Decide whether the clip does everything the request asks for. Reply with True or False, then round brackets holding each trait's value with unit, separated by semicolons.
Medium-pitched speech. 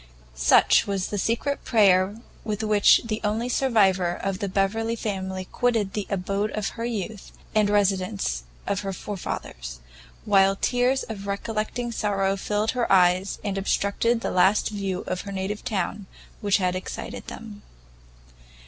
False (200 Hz)